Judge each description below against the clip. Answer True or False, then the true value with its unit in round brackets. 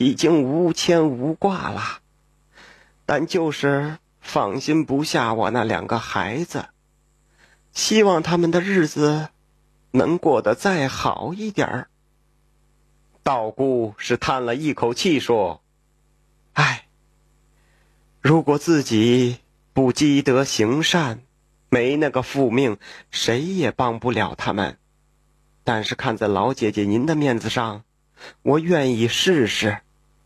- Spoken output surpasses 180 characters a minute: False (165 characters per minute)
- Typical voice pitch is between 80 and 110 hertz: False (135 Hz)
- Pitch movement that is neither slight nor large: False (5.7 semitones)